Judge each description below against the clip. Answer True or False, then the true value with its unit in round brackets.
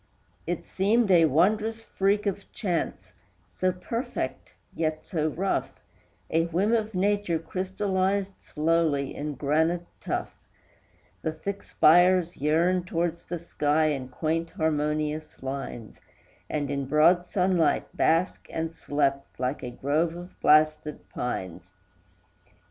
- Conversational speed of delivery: False (120 wpm)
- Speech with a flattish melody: False (3.6 semitones)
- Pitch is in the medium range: True (165 Hz)